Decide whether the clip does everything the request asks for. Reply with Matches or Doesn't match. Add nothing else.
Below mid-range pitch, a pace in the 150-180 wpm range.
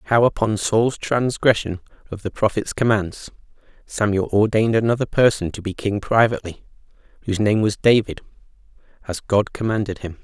Doesn't match